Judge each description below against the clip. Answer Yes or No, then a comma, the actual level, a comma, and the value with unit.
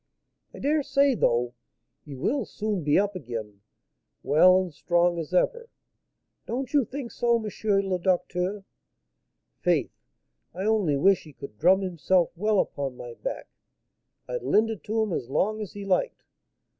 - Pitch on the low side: No, high, 190 Hz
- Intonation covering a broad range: Yes, wide, 5.7 semitones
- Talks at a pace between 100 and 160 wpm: Yes, average, 155 wpm